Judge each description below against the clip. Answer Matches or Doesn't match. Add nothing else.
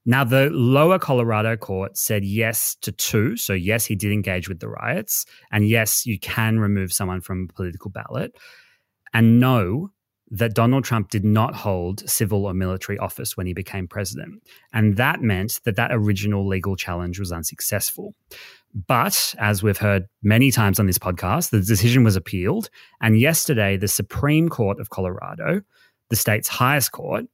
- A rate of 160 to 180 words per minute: Matches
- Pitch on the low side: Matches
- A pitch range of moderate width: Matches